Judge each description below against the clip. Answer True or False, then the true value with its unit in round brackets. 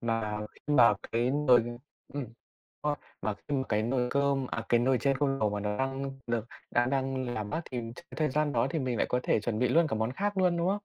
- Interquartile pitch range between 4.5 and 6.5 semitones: False (3.5 semitones)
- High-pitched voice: False (130 Hz)